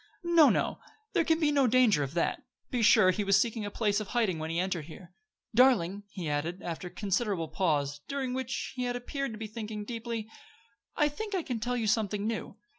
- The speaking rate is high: Yes, fast, 215 wpm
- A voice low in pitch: No, high, 215 Hz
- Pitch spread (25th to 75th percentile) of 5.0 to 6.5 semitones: Yes, average, 5.3 semitones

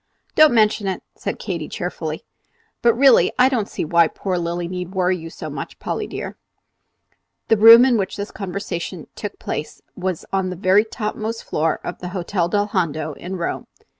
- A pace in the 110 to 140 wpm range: No, average, 175 wpm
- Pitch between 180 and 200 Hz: Yes, high, 190 Hz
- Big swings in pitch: No, average, 3.7 semitones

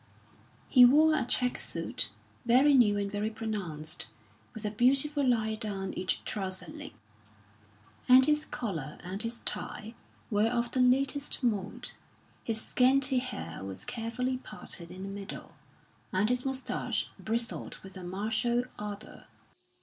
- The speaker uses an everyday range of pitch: Yes, average, 4.2 semitones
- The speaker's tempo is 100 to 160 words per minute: Yes, average, 140 wpm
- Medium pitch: No, high, 225 Hz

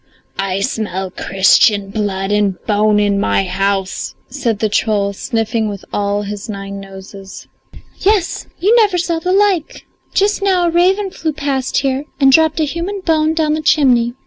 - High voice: Yes, high, 230 Hz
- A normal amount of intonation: No, wide, 8.4 semitones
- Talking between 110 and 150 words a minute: No, average, 165 wpm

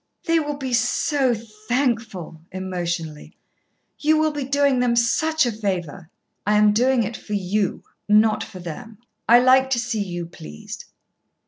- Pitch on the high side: Yes, high, 225 Hz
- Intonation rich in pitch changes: Yes, wide, 5.8 semitones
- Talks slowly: No, average, 150 wpm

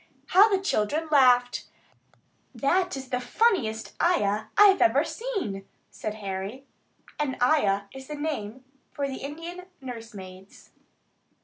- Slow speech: Yes, slow, 125 wpm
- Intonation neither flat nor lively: No, wide, 7.0 semitones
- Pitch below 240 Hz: No, very high, 265 Hz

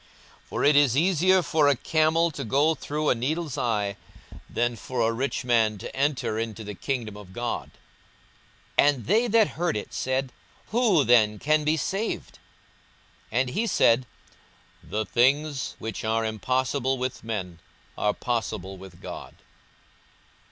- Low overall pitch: Yes, low, 130 Hz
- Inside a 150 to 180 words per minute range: Yes, average, 155 wpm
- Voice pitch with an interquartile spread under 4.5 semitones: No, wide, 5.5 semitones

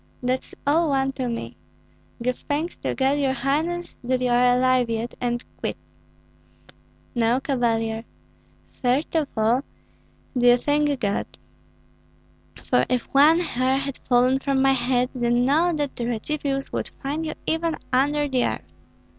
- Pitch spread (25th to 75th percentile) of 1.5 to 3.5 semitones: Yes, average, 2.9 semitones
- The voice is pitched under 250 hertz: No, very high, 265 Hz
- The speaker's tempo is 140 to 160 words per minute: Yes, average, 150 wpm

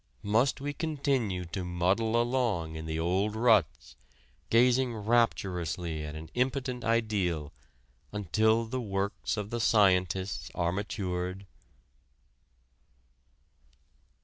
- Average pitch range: Yes, average, 4.8 semitones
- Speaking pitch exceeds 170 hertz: No, low, 100 Hz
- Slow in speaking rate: Yes, slow, 100 wpm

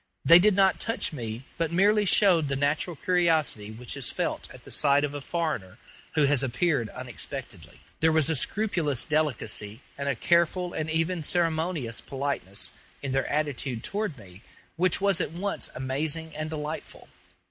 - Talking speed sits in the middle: Yes, average, 165 wpm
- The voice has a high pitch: No, medium, 155 Hz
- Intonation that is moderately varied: Yes, average, 4.1 semitones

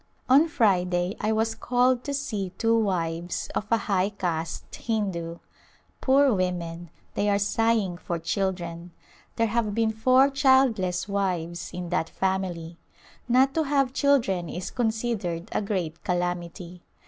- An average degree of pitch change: Yes, average, 4.6 semitones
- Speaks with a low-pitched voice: No, high, 195 Hz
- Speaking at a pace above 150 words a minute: No, slow, 135 wpm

